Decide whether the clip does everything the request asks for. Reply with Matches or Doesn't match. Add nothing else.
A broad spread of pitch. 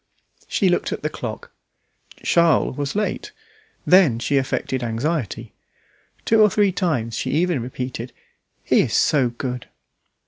Matches